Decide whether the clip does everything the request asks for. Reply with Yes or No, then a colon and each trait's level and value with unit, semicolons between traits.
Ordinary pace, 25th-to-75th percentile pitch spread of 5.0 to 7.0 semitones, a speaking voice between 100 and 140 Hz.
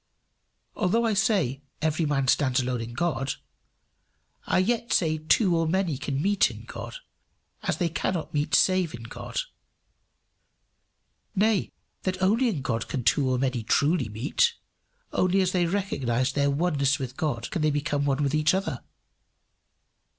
No: average, 155 wpm; wide, 5.6 semitones; medium, 155 Hz